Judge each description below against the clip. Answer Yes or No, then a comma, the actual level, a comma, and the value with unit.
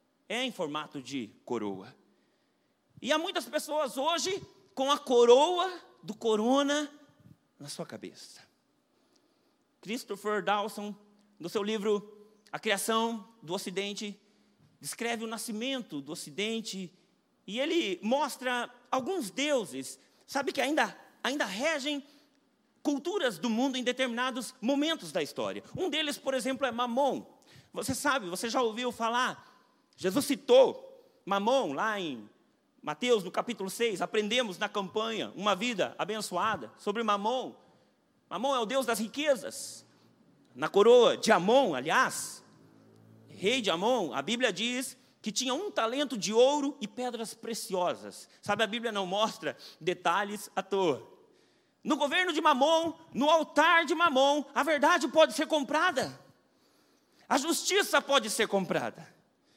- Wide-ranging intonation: Yes, wide, 5.7 semitones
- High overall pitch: Yes, very high, 250 Hz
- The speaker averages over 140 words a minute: No, average, 130 wpm